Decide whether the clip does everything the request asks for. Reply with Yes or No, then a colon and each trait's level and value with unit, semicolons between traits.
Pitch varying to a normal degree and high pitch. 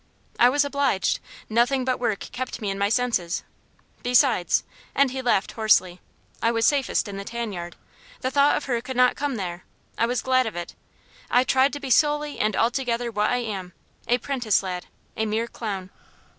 Yes: average, 4.1 semitones; high, 235 Hz